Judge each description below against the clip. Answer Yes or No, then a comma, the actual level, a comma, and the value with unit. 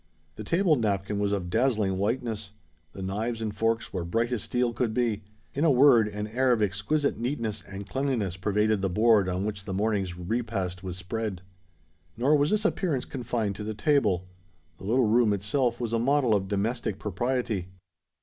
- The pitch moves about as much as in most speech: Yes, average, 3.6 semitones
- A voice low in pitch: Yes, low, 110 Hz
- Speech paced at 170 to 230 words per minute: Yes, average, 180 wpm